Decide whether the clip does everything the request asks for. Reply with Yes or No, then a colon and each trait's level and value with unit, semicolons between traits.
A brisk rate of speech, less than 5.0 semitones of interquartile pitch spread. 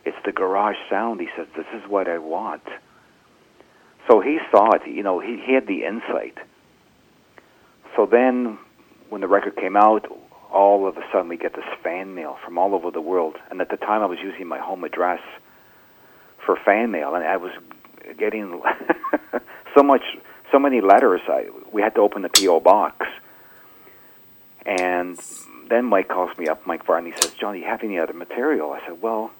No: average, 185 wpm; average, 3.8 semitones